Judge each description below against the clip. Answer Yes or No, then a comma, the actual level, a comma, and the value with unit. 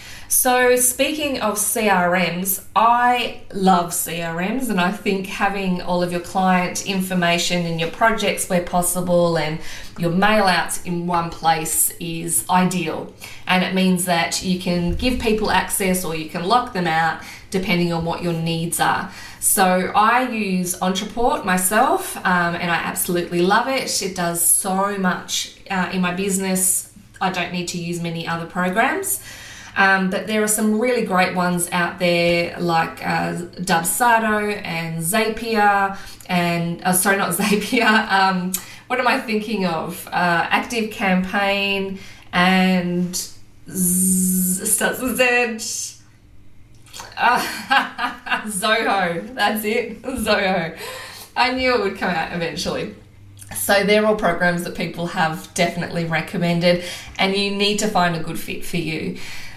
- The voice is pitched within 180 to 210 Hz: Yes, medium, 185 Hz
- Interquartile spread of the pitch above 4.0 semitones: No, average, 3.4 semitones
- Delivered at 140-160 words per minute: Yes, average, 145 wpm